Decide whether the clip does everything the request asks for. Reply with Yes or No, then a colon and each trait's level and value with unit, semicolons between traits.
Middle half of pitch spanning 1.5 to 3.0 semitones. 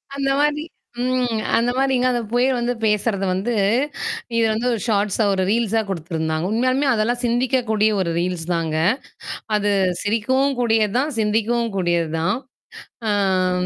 No: average, 4.3 semitones